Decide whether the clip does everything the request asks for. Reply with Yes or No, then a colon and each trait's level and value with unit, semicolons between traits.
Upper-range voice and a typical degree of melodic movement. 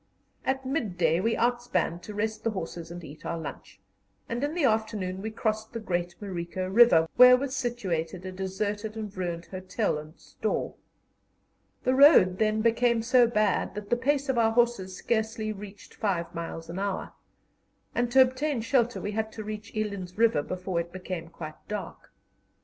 Yes: high, 210 Hz; average, 4.4 semitones